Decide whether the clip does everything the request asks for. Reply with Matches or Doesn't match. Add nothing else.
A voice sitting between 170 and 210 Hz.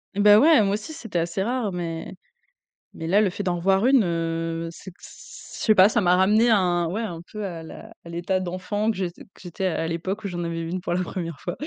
Matches